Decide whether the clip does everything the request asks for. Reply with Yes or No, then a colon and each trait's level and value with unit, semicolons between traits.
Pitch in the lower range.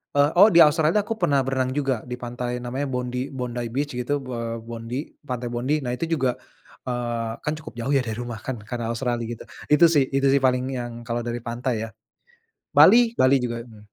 Yes: low, 125 Hz